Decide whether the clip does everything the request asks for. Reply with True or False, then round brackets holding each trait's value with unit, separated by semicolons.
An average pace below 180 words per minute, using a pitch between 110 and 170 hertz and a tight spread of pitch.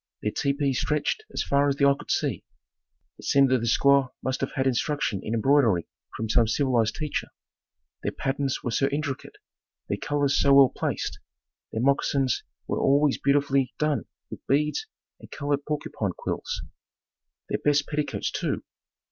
True (160 wpm; 140 Hz; 1.9 semitones)